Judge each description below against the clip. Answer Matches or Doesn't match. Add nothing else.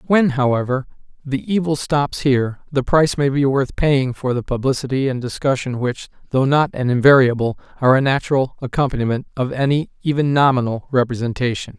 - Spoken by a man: Matches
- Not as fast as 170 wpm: Matches